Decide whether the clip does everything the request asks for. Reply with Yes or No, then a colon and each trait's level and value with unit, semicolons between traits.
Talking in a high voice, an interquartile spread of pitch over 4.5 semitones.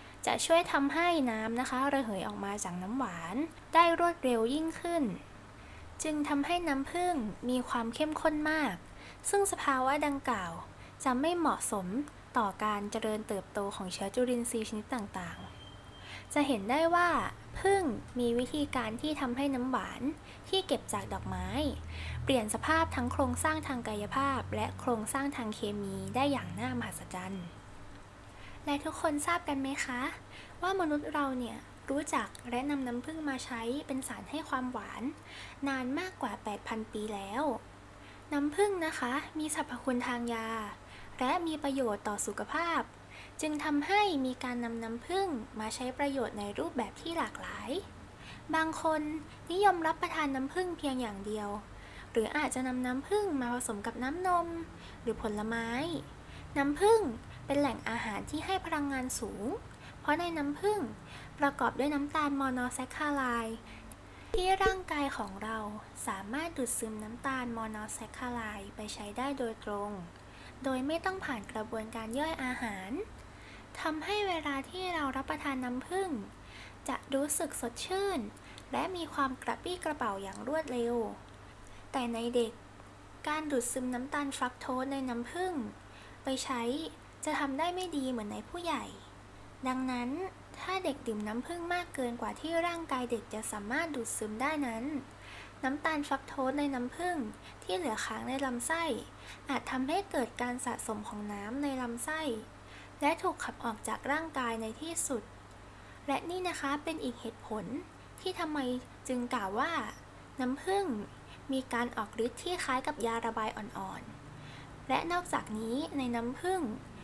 Yes: very high, 265 Hz; average, 5.1 semitones